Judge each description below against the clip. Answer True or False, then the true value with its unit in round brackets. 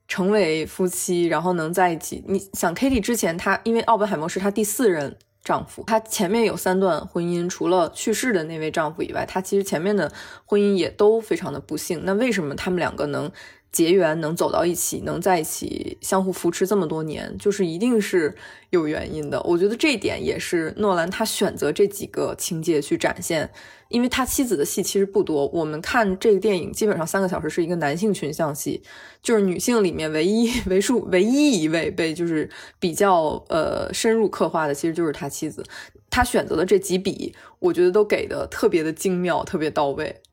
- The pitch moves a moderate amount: True (4.5 semitones)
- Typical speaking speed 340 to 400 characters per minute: False (315 characters per minute)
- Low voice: False (195 Hz)